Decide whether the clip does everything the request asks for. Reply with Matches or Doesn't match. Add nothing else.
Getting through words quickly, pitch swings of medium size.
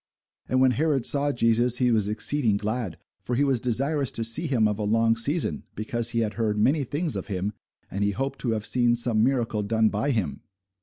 Matches